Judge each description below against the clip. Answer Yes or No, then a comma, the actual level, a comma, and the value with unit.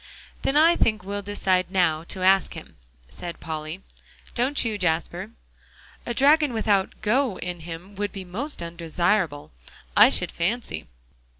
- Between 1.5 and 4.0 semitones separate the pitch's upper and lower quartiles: No, average, 4.6 semitones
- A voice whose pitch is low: No, high, 190 Hz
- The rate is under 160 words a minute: Yes, average, 140 wpm